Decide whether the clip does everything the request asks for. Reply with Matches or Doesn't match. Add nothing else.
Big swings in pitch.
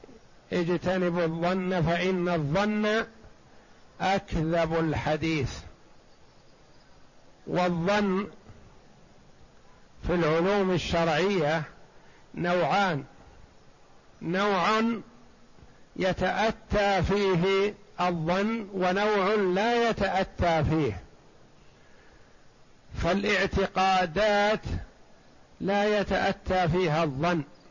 Doesn't match